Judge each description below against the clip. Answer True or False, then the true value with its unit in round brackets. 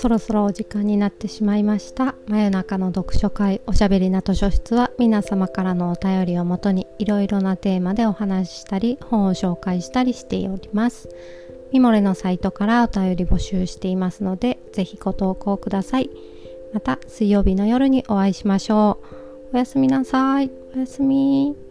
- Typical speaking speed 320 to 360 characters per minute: False (370 characters per minute)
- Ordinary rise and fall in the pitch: True (4.0 semitones)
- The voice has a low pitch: False (205 Hz)